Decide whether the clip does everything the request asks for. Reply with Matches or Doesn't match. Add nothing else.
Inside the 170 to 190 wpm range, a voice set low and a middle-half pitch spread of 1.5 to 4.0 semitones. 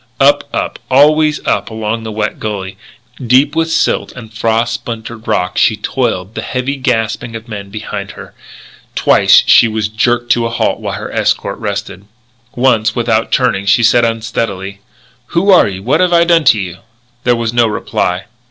Matches